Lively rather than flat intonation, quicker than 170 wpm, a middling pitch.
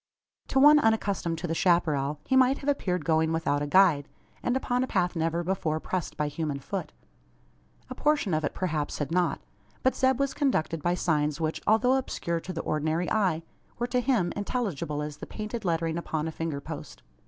Yes: wide, 6.2 semitones; average, 195 wpm; medium, 170 Hz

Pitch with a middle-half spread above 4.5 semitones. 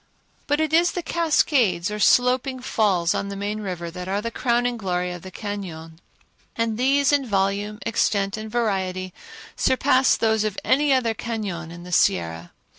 Yes: average, 5.2 semitones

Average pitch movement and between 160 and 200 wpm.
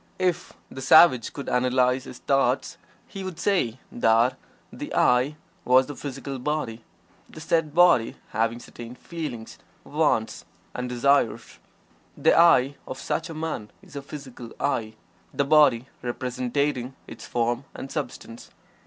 No: average, 3.7 semitones; slow, 135 wpm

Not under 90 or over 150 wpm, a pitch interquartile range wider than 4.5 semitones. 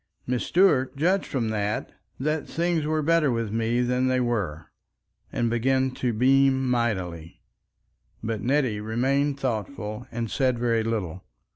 No: average, 140 wpm; average, 3.5 semitones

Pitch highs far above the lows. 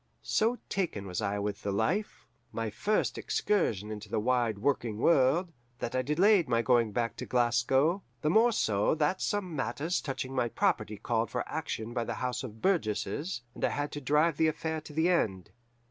Yes: wide, 6.5 semitones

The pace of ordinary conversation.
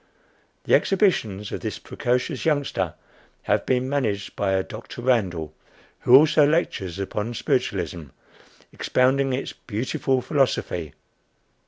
No: slow, 115 wpm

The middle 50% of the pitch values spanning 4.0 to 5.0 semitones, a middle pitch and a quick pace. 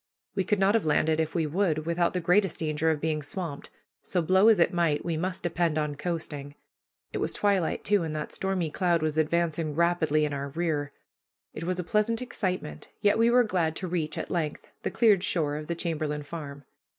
No: average, 3.2 semitones; medium, 165 Hz; fast, 210 wpm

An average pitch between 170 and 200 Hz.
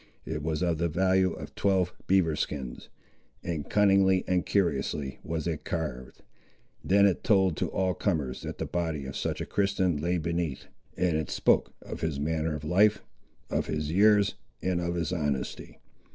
No: very low, 85 Hz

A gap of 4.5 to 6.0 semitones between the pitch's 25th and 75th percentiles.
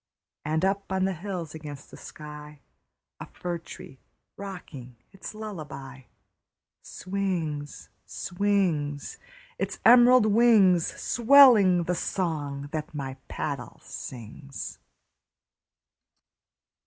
Yes: average, 5.2 semitones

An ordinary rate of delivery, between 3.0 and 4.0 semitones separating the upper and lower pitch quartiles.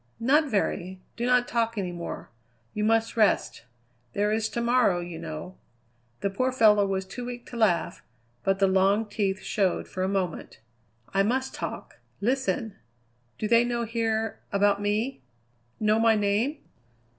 Yes: average, 155 wpm; average, 3.3 semitones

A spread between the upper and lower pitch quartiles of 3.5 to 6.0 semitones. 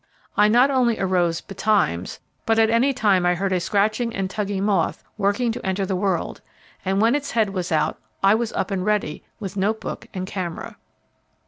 No: average, 2.9 semitones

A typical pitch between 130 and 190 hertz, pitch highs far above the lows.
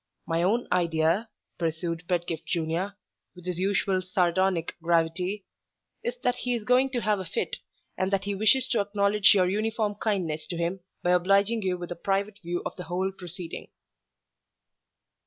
No: medium, 185 Hz; average, 3.0 semitones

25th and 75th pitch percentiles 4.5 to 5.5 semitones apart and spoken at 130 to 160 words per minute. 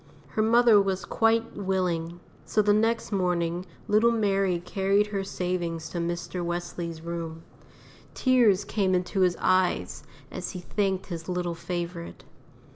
No: average, 3.0 semitones; slow, 135 wpm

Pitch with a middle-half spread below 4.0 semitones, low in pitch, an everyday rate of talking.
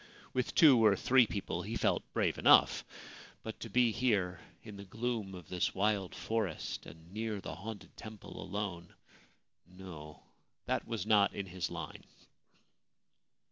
Yes: average, 3.6 semitones; low, 100 Hz; average, 150 wpm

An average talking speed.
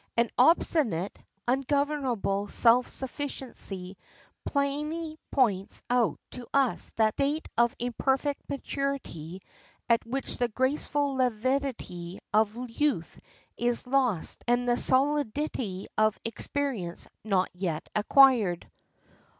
No: slow, 100 wpm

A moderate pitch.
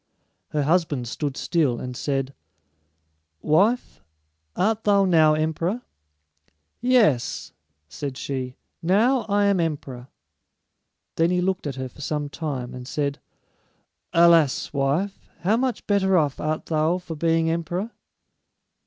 Yes: medium, 160 Hz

